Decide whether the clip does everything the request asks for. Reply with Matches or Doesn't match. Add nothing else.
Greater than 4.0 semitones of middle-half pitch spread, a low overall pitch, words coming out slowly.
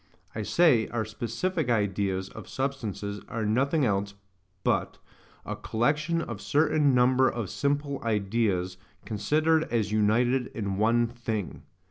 Matches